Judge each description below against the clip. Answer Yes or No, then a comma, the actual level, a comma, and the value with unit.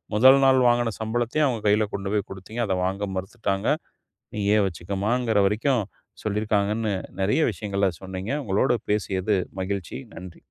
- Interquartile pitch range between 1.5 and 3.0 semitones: Yes, average, 2.7 semitones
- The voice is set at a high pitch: No, low, 105 Hz